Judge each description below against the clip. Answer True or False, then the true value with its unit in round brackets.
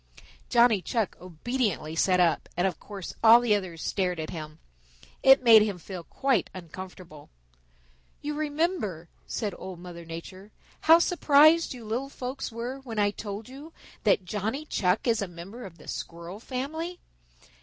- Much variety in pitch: True (6.3 semitones)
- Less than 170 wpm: True (155 wpm)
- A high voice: True (210 Hz)